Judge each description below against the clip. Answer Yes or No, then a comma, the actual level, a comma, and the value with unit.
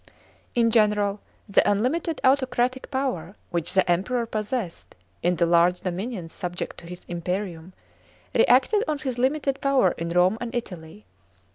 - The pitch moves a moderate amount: No, wide, 6.2 semitones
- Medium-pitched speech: No, high, 210 Hz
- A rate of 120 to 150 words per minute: Yes, average, 140 wpm